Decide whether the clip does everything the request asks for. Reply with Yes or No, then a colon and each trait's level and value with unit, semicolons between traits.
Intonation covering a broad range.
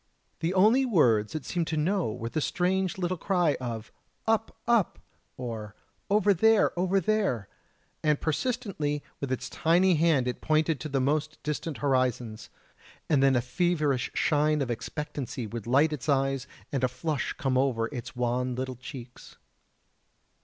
Yes: wide, 5.7 semitones